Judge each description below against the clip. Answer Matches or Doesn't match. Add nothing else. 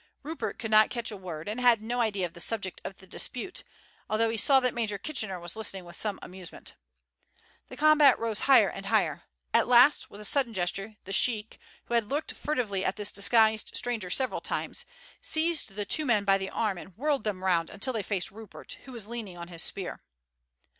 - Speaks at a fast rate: Matches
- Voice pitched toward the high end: Matches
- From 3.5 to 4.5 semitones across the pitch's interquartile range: Matches